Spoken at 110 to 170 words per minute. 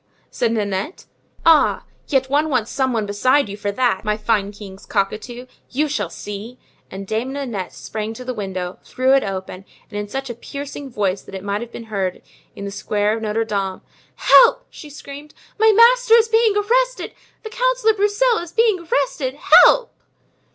No: average, 180 wpm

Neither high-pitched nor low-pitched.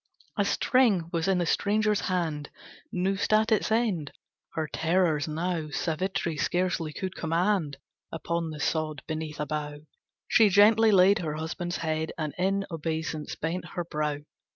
Yes: medium, 170 Hz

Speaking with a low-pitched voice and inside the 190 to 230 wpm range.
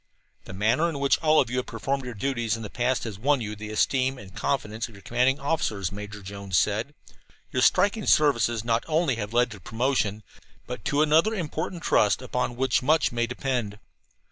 Yes: low, 120 Hz; average, 195 wpm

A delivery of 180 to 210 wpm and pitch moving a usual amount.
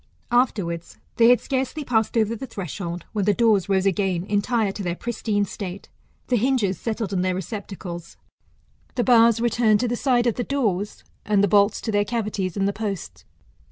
Yes: average, 185 wpm; average, 3.5 semitones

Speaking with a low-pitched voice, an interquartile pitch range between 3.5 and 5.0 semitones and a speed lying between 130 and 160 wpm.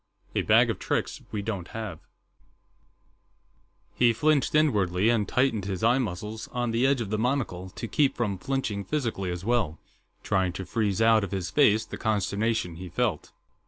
No: low, 110 Hz; average, 4.1 semitones; average, 170 wpm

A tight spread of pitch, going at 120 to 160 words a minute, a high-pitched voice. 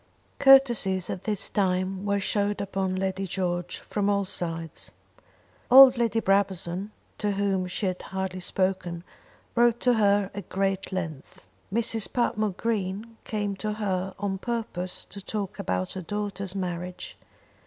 Yes: narrow, 2.1 semitones; average, 140 wpm; high, 195 Hz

